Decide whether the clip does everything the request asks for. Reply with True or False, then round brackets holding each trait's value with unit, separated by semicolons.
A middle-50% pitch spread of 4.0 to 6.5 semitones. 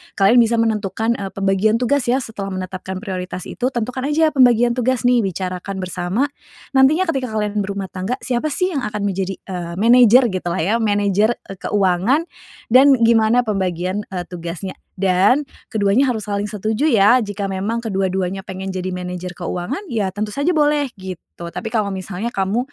True (4.3 semitones)